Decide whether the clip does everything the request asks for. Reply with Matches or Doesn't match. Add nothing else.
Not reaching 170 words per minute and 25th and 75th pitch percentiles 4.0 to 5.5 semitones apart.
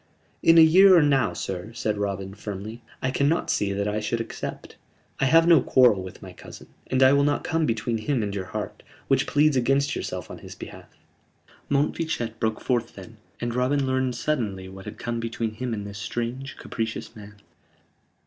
Doesn't match